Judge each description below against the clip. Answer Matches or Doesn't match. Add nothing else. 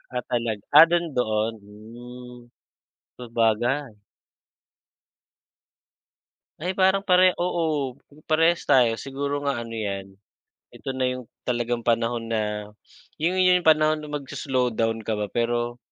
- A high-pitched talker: Doesn't match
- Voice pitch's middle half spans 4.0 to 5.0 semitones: Matches